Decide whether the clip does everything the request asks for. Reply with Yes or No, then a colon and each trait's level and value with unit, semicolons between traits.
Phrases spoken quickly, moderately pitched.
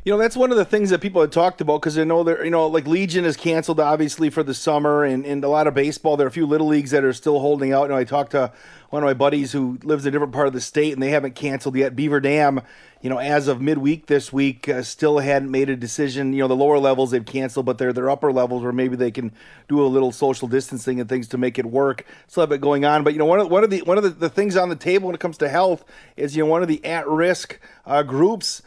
Yes: fast, 300 wpm; medium, 145 Hz